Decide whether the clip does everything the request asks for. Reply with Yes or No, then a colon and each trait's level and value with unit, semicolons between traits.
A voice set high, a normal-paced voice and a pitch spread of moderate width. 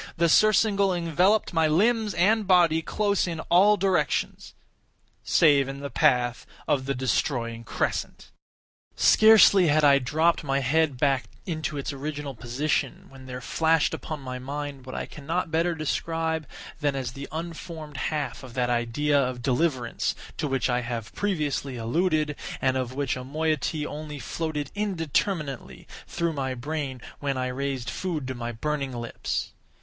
No: medium, 145 Hz; average, 150 wpm; average, 4.1 semitones